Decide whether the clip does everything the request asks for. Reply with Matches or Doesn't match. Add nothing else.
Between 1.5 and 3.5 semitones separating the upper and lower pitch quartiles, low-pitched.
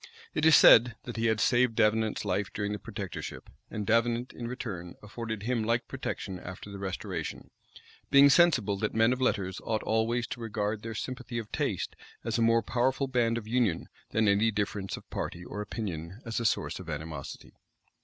Matches